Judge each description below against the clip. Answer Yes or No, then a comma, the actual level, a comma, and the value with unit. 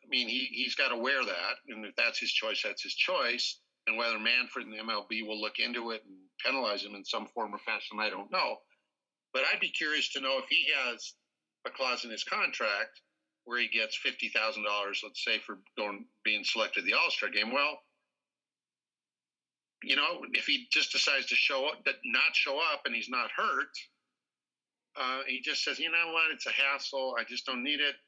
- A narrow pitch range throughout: No, average, 4.0 semitones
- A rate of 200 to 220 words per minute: Yes, fast, 205 wpm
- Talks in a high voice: No, low, 125 Hz